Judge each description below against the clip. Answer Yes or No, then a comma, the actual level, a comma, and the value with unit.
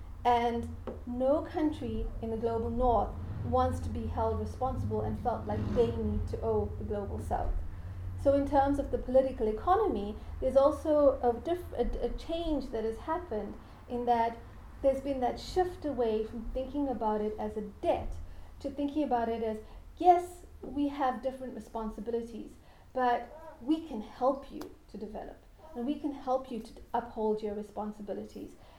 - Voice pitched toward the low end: No, high, 235 Hz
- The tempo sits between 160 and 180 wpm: Yes, average, 165 wpm